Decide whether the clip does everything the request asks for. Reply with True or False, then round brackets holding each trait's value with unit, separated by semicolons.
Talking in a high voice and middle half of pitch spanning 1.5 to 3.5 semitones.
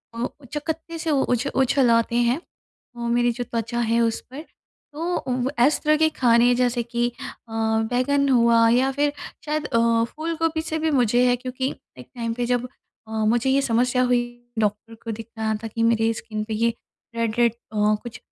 True (240 Hz; 2.8 semitones)